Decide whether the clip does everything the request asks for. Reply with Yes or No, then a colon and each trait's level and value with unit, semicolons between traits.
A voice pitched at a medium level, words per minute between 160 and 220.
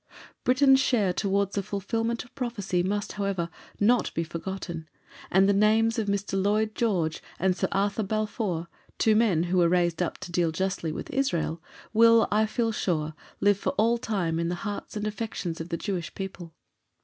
No: high, 200 Hz; average, 180 wpm